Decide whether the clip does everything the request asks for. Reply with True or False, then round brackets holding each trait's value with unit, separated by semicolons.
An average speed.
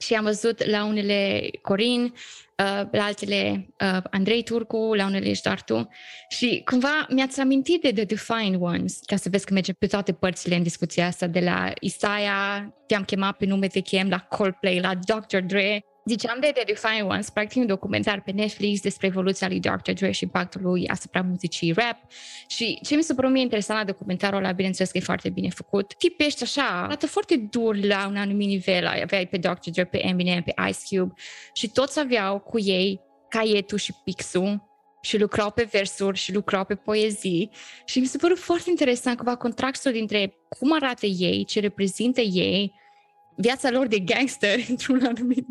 False (185 wpm)